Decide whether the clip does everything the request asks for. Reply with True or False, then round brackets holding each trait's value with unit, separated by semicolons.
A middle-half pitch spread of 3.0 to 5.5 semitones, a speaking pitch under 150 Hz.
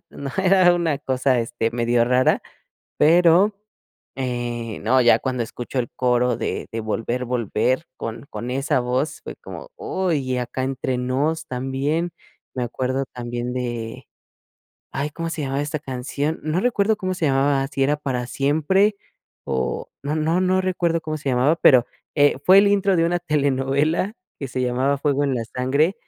True (4.5 semitones; 135 Hz)